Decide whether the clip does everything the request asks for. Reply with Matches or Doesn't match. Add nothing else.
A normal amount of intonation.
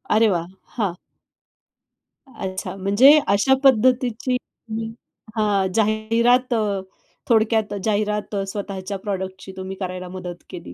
Matches